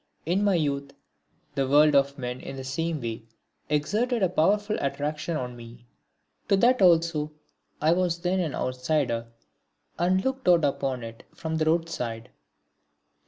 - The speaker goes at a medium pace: Yes, average, 150 wpm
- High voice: No, medium, 155 Hz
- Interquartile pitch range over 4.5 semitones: Yes, average, 4.9 semitones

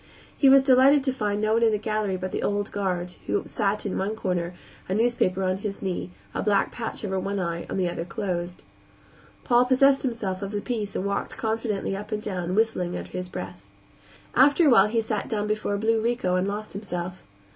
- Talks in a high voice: Yes, high, 205 Hz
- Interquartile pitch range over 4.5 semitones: No, average, 3.3 semitones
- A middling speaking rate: No, fast, 215 wpm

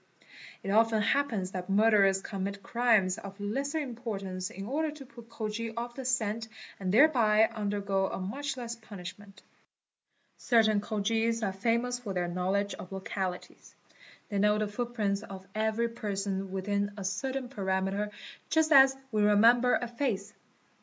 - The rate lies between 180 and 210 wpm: No, average, 155 wpm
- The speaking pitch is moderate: No, high, 210 Hz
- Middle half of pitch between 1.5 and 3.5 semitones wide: Yes, average, 3.2 semitones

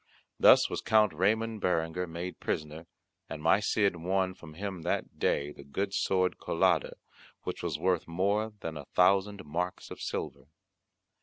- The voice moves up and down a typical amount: Yes, average, 3.4 semitones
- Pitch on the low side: Yes, very low, 90 Hz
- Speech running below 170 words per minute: Yes, average, 155 wpm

